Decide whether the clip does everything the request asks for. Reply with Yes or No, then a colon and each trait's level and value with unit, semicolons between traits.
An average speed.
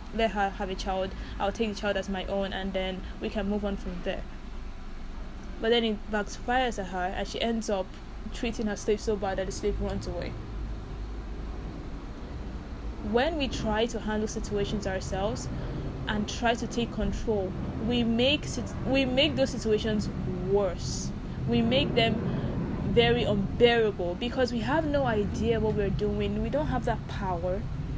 Yes: average, 165 wpm